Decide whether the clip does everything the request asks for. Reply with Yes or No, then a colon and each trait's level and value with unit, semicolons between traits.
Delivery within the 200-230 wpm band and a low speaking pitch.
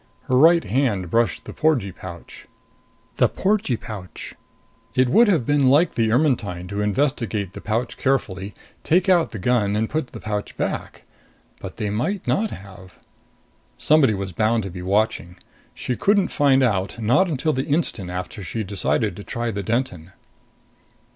No: average, 160 wpm; low, 115 Hz